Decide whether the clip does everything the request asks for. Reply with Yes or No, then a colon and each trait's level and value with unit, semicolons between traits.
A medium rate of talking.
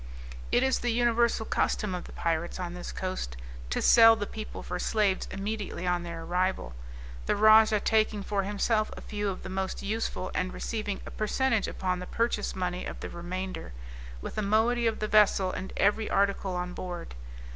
Yes: average, 185 wpm